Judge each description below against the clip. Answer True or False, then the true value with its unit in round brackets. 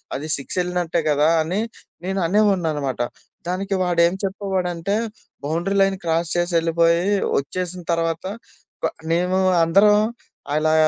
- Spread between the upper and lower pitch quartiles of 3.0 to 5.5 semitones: False (2.4 semitones)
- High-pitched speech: False (175 Hz)